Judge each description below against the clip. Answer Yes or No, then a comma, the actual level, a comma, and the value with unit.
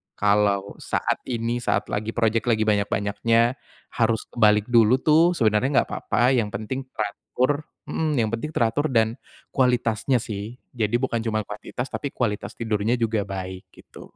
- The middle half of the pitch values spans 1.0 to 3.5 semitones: Yes, average, 2.8 semitones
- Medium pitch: No, low, 115 Hz